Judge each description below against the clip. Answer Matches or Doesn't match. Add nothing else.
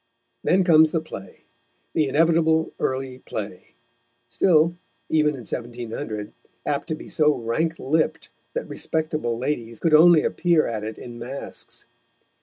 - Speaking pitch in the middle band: Matches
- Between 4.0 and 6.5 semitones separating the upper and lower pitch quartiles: Matches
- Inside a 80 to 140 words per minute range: Matches